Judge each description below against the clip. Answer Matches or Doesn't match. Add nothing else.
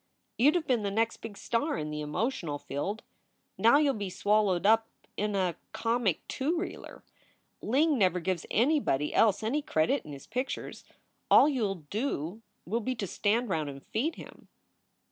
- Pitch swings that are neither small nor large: Doesn't match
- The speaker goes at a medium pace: Matches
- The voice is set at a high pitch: Matches